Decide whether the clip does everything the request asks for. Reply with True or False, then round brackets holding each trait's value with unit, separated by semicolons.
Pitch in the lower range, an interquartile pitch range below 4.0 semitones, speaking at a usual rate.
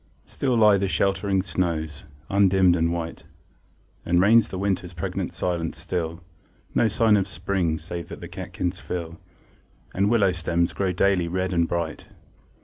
True (90 Hz; 2.6 semitones; 150 wpm)